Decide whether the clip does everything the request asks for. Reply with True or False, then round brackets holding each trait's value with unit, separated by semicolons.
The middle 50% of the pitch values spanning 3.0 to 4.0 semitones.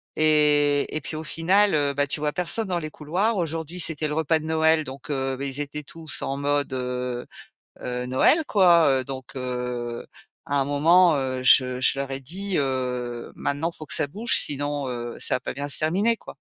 True (3.5 semitones)